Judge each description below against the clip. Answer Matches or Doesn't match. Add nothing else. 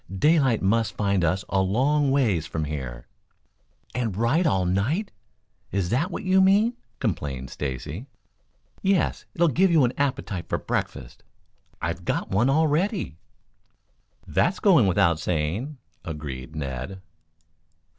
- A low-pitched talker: Matches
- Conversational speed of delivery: Doesn't match